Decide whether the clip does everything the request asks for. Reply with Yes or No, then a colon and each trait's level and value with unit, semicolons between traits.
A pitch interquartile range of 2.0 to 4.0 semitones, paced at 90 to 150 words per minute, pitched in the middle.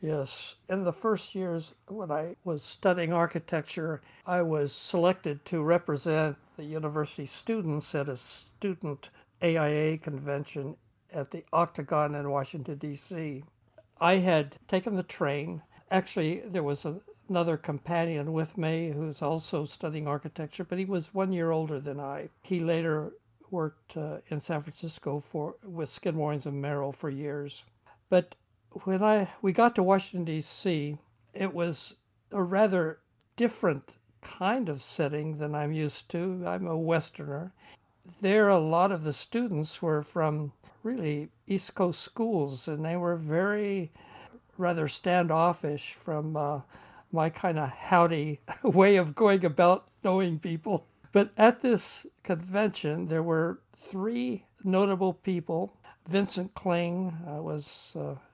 Yes: average, 3.7 semitones; slow, 135 wpm; medium, 165 Hz